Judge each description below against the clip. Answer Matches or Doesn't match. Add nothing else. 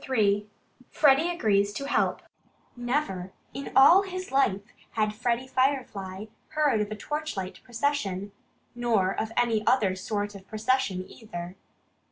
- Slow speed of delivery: Matches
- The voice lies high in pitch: Matches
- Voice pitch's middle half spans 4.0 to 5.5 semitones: Matches